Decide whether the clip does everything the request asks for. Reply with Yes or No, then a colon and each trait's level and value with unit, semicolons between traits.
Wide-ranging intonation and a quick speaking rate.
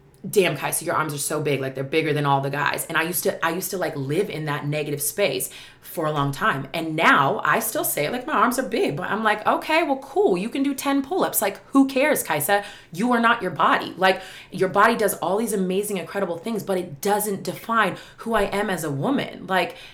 Yes: wide, 6.1 semitones; fast, 245 wpm